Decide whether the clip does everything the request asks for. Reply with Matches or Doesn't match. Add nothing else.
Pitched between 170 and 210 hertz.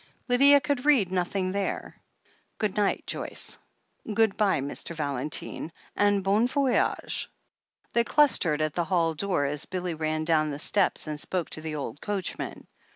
Matches